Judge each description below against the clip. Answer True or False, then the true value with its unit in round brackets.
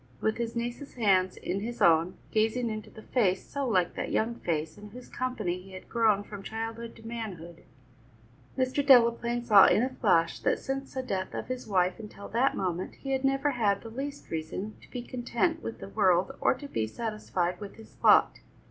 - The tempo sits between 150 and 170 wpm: False (200 wpm)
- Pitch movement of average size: True (4.6 semitones)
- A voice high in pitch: True (220 Hz)